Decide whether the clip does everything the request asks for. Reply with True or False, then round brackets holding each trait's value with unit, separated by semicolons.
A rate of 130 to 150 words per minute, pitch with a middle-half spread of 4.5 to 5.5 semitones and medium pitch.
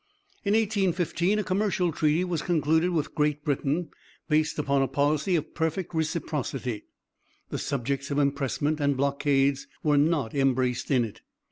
False (145 wpm; 3.4 semitones; 150 Hz)